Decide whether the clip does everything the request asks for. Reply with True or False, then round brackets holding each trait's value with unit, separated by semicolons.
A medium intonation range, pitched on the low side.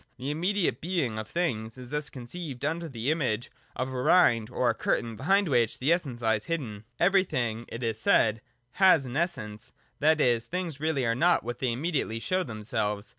False (6.3 semitones; 130 Hz)